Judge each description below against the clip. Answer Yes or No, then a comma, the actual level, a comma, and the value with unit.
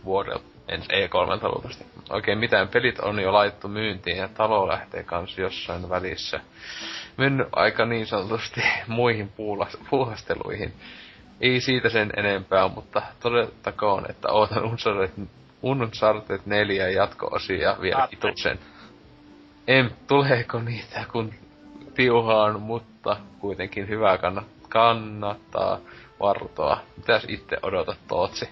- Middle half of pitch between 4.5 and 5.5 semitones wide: No, average, 3.2 semitones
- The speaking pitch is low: Yes, low, 110 Hz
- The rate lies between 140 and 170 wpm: No, average, 110 wpm